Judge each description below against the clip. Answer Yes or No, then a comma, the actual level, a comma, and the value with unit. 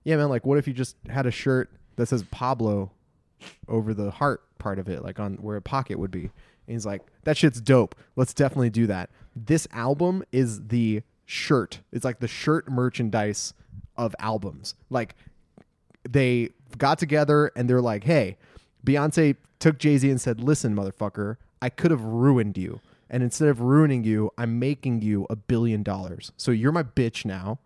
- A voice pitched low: Yes, low, 120 Hz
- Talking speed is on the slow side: No, average, 185 wpm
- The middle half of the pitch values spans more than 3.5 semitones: Yes, average, 4.5 semitones